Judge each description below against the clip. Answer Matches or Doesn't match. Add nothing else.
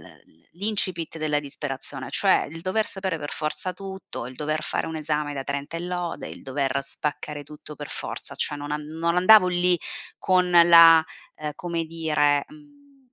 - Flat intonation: Doesn't match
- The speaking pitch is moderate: Matches